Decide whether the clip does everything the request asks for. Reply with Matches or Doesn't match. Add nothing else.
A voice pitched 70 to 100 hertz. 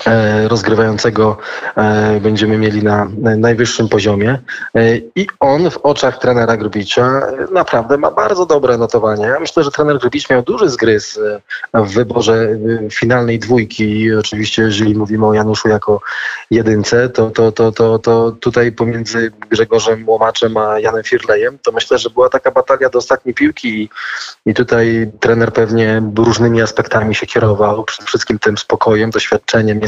Doesn't match